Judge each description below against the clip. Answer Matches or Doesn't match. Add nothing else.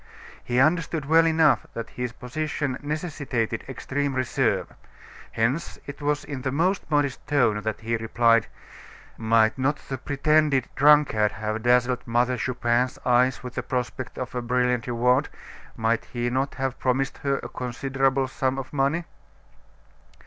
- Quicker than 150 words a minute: Doesn't match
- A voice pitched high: Doesn't match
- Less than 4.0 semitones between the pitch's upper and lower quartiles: Matches